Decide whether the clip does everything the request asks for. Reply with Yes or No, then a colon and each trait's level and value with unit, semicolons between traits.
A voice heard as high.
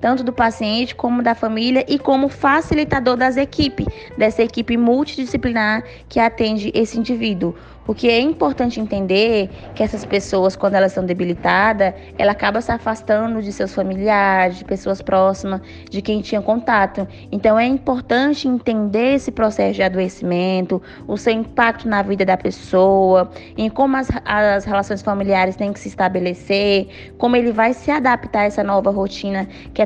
Yes: high, 215 Hz